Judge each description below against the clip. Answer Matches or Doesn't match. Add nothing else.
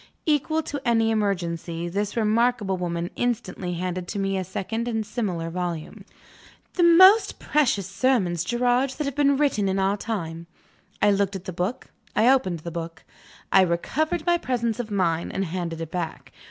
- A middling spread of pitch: Doesn't match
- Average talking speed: Matches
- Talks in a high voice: Matches